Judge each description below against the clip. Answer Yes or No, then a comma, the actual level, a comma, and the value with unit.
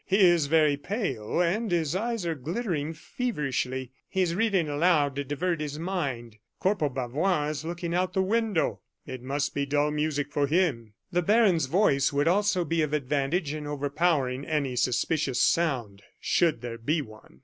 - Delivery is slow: No, average, 170 wpm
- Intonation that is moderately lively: Yes, average, 4.2 semitones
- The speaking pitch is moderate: Yes, medium, 150 Hz